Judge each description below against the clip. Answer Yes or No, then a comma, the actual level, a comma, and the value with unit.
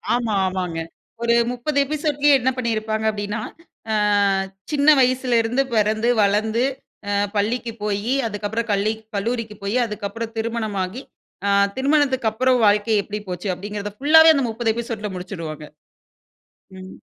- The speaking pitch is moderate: No, high, 220 Hz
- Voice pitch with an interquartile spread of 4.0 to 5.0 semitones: No, average, 3.3 semitones